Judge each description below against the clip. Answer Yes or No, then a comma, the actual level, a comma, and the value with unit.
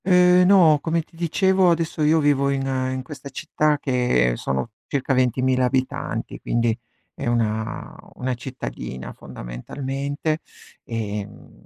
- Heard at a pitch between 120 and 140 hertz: Yes, low, 135 Hz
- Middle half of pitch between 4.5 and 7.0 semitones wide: Yes, average, 4.8 semitones